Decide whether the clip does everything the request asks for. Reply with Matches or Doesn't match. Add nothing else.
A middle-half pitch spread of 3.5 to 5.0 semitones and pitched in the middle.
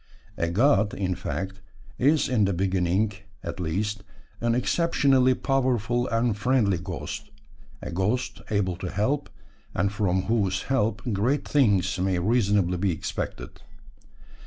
Doesn't match